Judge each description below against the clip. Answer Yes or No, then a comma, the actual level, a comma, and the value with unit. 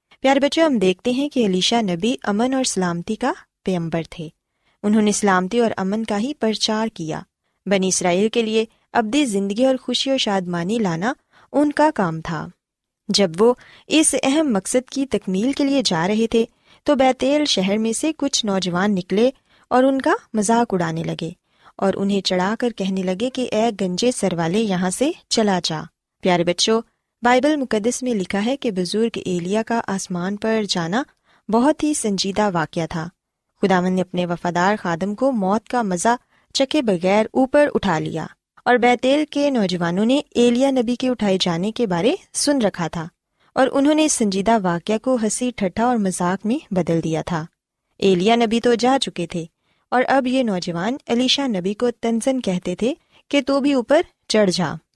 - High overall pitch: Yes, high, 220 Hz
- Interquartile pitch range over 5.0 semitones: Yes, wide, 5.4 semitones